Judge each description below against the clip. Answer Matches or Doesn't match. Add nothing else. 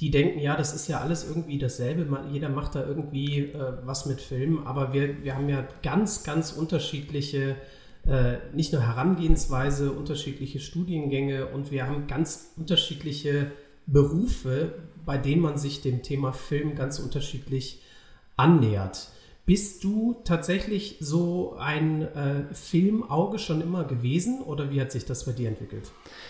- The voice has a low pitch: Doesn't match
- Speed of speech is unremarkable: Matches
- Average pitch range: Matches